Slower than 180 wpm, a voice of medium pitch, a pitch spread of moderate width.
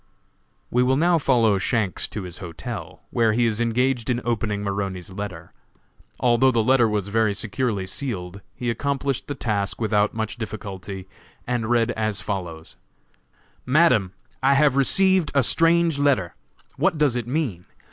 No: average, 150 wpm; low, 115 Hz; average, 4.7 semitones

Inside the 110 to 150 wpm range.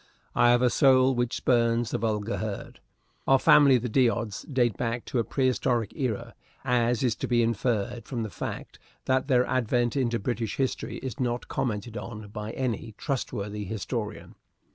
No: average, 165 wpm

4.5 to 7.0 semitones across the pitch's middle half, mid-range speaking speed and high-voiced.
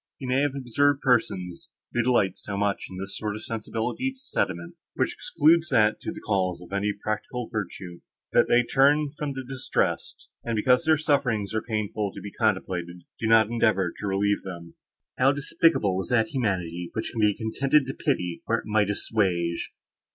No: average, 5.2 semitones; average, 185 wpm; low, 110 Hz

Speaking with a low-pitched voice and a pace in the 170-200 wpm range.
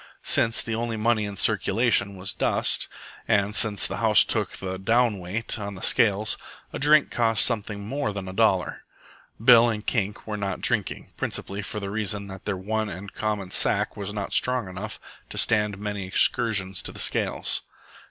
Yes: low, 105 Hz; average, 180 wpm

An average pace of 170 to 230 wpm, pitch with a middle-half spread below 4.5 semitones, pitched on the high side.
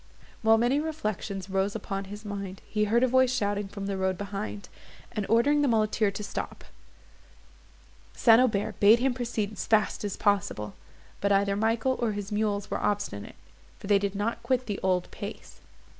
Yes: average, 175 wpm; narrow, 2.5 semitones; high, 205 Hz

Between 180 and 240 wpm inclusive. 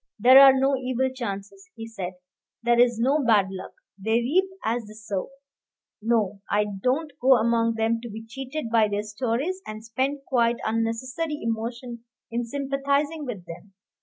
No: average, 165 wpm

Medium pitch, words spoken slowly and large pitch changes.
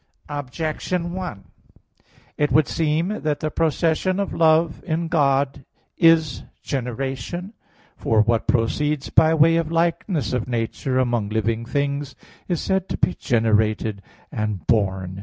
Yes: medium, 145 Hz; slow, 130 wpm; wide, 6.1 semitones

